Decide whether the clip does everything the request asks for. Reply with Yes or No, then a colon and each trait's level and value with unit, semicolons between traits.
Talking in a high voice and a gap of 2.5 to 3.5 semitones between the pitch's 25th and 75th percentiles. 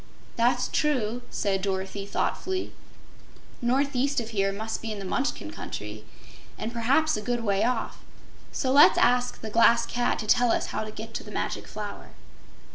Yes: high, 230 Hz; average, 3.1 semitones